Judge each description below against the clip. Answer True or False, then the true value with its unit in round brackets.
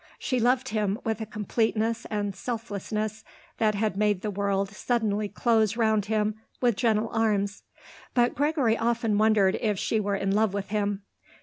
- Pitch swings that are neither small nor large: False (1.9 semitones)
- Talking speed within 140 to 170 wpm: True (165 wpm)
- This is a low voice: False (215 Hz)